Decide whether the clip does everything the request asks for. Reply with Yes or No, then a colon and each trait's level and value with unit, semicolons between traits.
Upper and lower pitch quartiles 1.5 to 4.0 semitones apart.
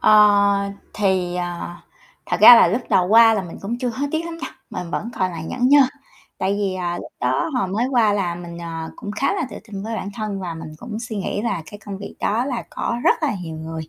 No: average, 4.6 semitones